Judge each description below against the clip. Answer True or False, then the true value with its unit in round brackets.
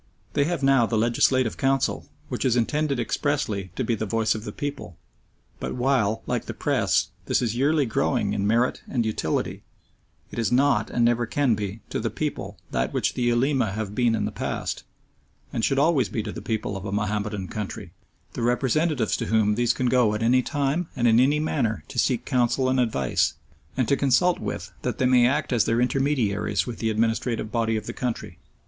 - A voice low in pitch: True (120 Hz)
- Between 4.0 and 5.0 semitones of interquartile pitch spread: False (3.5 semitones)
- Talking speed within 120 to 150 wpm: False (205 wpm)